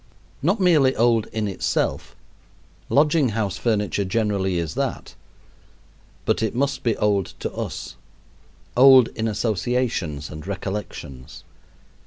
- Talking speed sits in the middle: No, slow, 115 wpm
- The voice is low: Yes, low, 110 Hz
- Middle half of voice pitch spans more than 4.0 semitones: Yes, average, 4.6 semitones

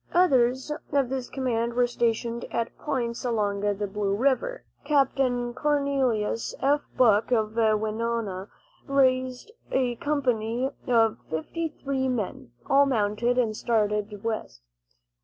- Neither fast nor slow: No, slow, 120 wpm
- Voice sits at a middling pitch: No, high, 235 Hz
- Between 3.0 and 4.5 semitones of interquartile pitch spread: Yes, average, 3.6 semitones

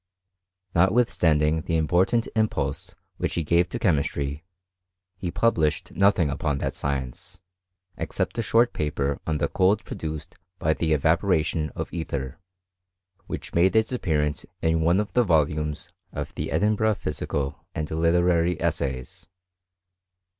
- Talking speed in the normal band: No, slow, 130 wpm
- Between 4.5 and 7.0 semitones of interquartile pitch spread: No, average, 3.8 semitones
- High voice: No, very low, 80 Hz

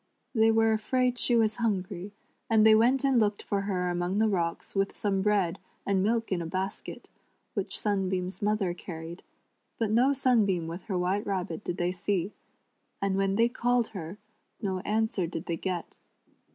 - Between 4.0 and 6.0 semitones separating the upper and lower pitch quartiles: No, average, 3.4 semitones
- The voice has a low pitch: No, high, 200 Hz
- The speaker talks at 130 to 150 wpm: No, average, 180 wpm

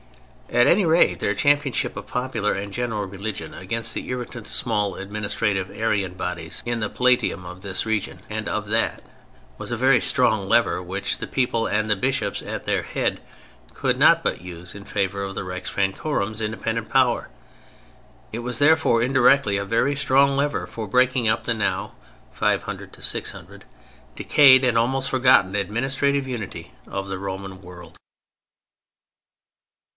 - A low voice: Yes, low, 110 Hz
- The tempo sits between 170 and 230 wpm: No, average, 155 wpm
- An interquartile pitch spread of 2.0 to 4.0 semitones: No, average, 4.5 semitones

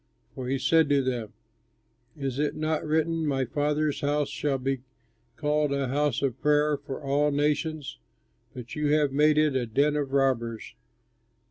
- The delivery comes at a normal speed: Yes, average, 155 wpm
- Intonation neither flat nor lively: No, narrow, 2.0 semitones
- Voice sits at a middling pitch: Yes, medium, 145 Hz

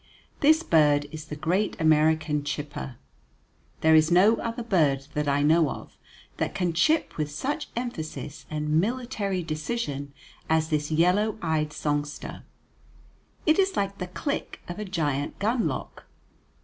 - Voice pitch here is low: No, medium, 160 Hz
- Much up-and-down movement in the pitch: Yes, wide, 5.8 semitones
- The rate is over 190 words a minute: No, average, 140 wpm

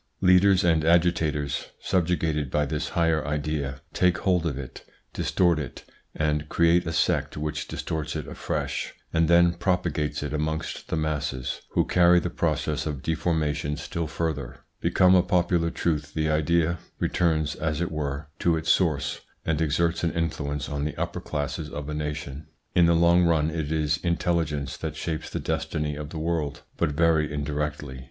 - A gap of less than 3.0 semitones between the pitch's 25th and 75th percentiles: Yes, narrow, 2.4 semitones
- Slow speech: No, average, 165 wpm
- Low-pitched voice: Yes, very low, 80 Hz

